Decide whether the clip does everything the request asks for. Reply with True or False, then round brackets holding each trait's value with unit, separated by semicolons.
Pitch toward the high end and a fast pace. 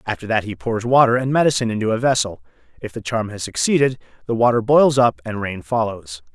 False (115 Hz; 210 wpm)